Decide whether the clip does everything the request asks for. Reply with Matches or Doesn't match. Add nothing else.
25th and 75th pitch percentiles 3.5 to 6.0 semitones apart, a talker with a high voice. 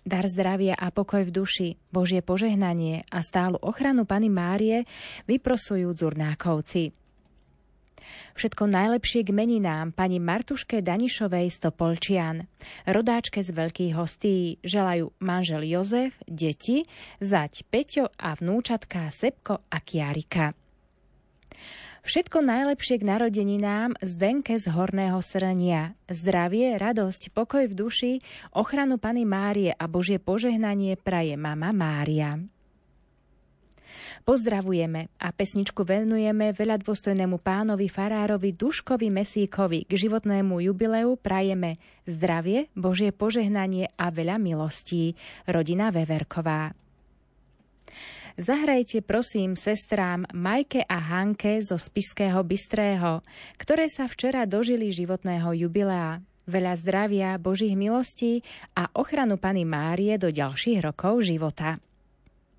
Matches